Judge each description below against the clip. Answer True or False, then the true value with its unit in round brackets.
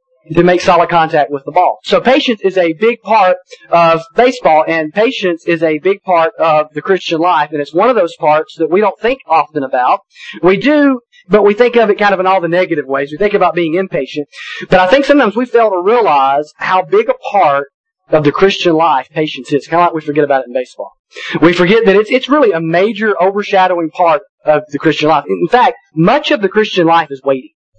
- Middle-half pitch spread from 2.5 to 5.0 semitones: False (5.4 semitones)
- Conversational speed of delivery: False (230 wpm)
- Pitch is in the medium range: True (180 Hz)